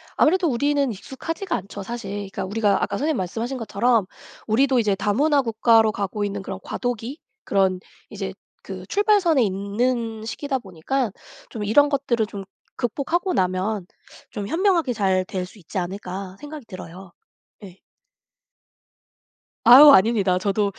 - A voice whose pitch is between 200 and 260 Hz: Yes, high, 220 Hz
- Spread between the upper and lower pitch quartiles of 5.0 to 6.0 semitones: Yes, wide, 5.6 semitones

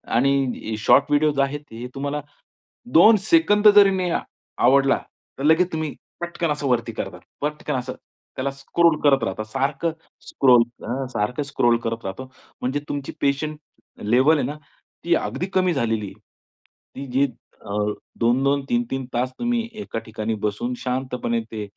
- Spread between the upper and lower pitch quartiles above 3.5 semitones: Yes, average, 4.1 semitones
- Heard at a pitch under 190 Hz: Yes, medium, 140 Hz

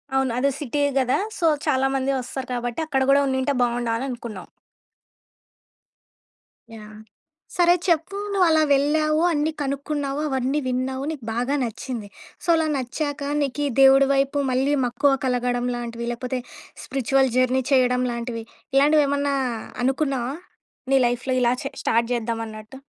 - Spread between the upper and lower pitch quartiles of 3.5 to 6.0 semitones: No, average, 2.7 semitones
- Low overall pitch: No, very high, 265 Hz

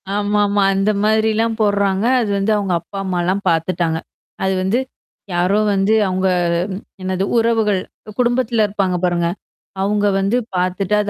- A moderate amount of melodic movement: No, narrow, 2.3 semitones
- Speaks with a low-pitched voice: No, high, 200 Hz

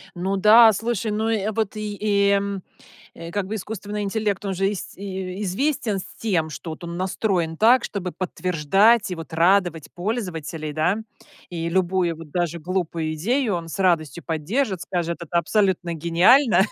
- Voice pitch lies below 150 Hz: No, medium, 185 Hz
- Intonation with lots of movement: No, average, 3.7 semitones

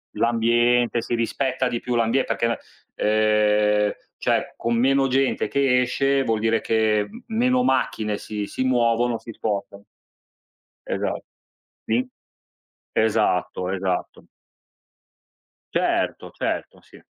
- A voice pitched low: Yes, low, 115 Hz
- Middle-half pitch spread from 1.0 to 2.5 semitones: No, average, 2.9 semitones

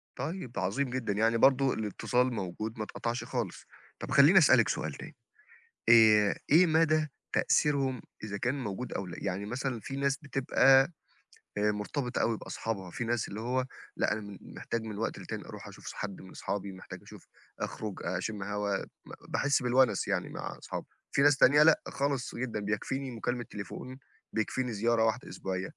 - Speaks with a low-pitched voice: Yes, low, 115 Hz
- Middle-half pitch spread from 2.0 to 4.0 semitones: No, average, 4.4 semitones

